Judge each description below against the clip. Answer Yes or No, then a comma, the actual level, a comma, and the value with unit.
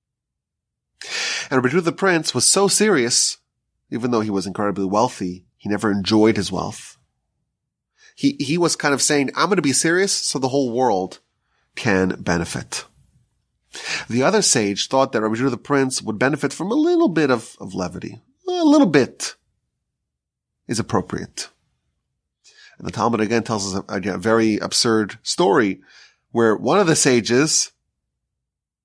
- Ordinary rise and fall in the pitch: No, wide, 7.0 semitones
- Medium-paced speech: Yes, average, 150 wpm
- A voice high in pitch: No, low, 125 Hz